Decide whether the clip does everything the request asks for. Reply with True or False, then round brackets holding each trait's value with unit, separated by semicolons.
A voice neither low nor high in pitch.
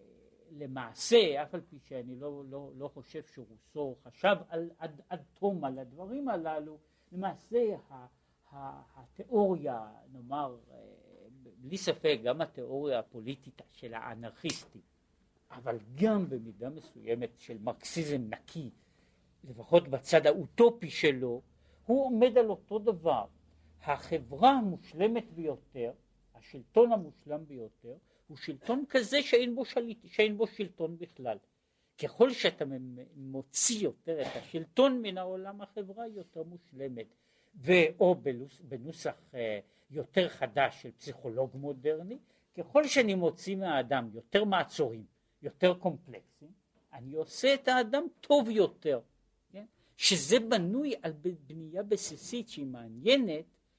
True (160 Hz)